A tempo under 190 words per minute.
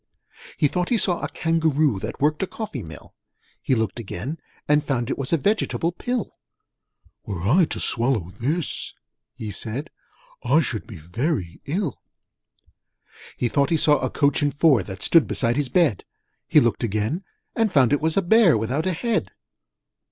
Yes: average, 175 wpm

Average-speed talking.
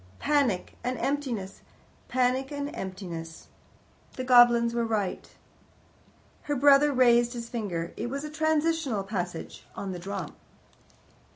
No: slow, 120 wpm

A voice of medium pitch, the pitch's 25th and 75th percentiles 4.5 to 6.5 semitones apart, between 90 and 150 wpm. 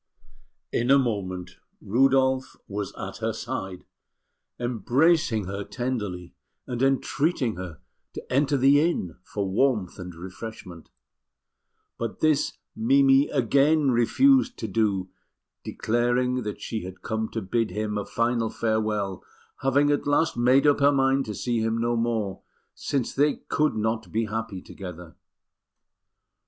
No: low, 115 Hz; average, 4.8 semitones; slow, 135 wpm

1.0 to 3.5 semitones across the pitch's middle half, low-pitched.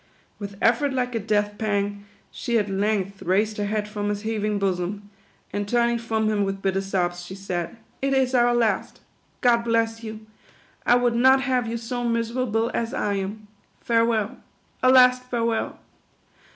No: average, 2.7 semitones; high, 220 Hz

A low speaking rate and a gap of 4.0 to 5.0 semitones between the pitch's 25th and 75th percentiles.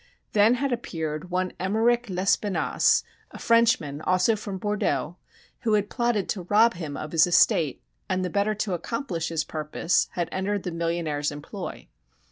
No: average, 155 wpm; average, 4.4 semitones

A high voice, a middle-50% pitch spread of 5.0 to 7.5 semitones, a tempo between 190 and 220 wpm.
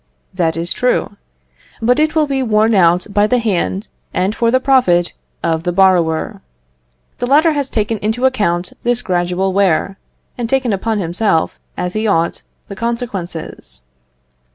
No: high, 205 Hz; wide, 5.4 semitones; average, 155 wpm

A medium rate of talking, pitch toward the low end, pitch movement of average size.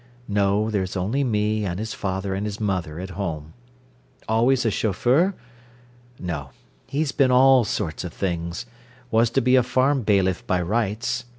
Yes: average, 155 wpm; low, 105 Hz; average, 4.6 semitones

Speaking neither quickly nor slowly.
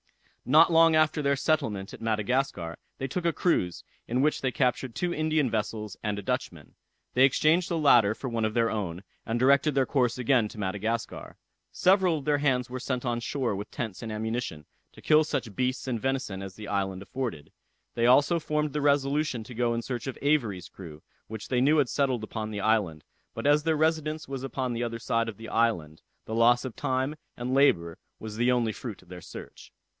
No: fast, 210 wpm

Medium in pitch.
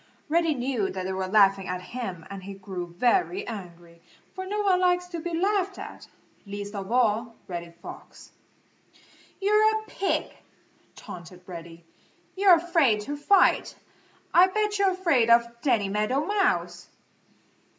No: high, 240 Hz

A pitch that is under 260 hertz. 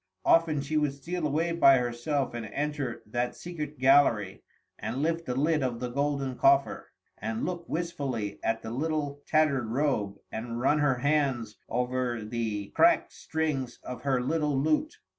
Yes: medium, 140 Hz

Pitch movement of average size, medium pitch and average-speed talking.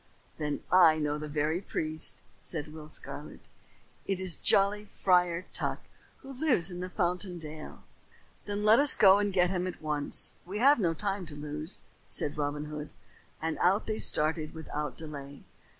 Yes: average, 4.3 semitones; medium, 170 Hz; average, 165 wpm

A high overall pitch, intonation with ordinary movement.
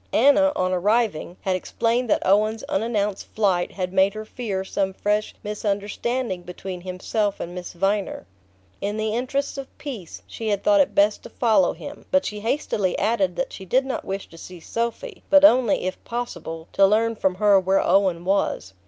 Yes: high, 205 Hz; average, 3.7 semitones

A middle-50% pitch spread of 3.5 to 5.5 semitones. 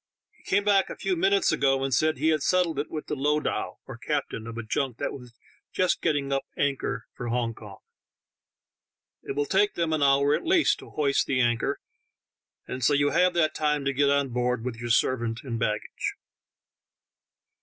Yes: average, 4.1 semitones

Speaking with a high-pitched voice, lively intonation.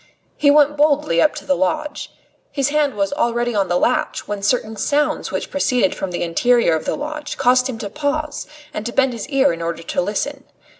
Yes: very high, 250 Hz; wide, 6.4 semitones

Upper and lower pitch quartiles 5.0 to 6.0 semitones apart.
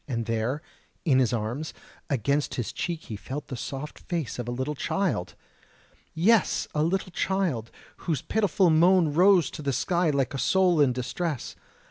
Yes: wide, 5.6 semitones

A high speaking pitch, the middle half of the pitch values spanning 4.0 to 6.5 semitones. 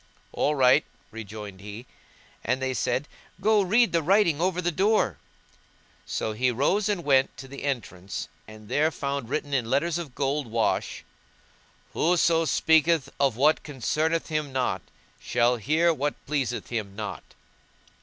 No: medium, 140 Hz; average, 5.3 semitones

